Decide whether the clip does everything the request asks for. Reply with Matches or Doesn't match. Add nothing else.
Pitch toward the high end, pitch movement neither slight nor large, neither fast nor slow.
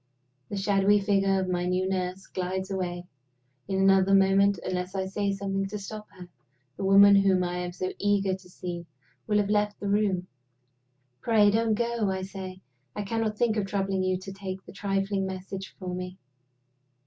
Doesn't match